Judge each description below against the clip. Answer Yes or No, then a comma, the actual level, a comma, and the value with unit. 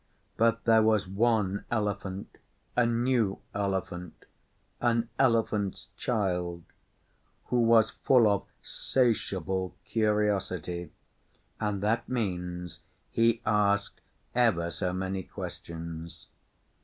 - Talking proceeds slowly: Yes, slow, 95 wpm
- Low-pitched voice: Yes, low, 100 Hz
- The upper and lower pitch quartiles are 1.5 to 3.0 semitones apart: No, average, 3.7 semitones